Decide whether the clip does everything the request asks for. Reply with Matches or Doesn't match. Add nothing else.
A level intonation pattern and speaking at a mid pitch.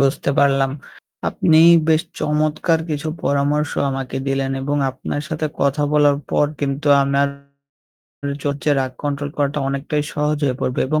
Matches